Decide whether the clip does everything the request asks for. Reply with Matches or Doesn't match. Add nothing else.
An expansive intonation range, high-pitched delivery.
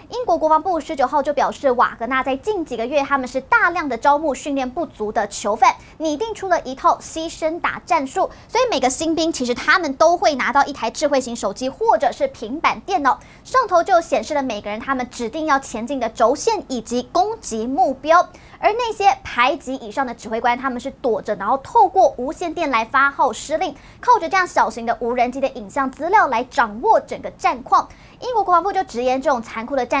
Matches